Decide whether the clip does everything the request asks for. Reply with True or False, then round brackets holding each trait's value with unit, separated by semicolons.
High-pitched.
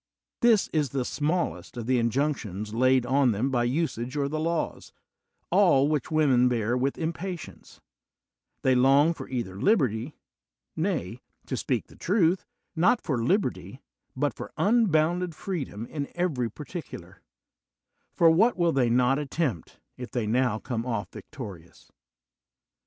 False (135 Hz)